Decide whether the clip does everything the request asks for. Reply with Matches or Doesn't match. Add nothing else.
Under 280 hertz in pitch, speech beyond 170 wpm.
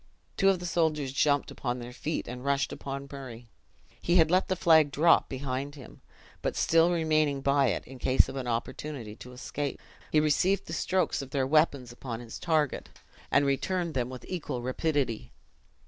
Matches